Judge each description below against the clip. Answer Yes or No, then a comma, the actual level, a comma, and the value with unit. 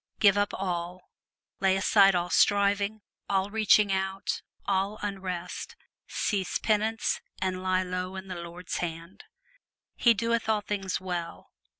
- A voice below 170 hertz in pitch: No, high, 195 Hz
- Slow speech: Yes, slow, 130 wpm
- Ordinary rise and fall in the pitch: No, narrow, 2.0 semitones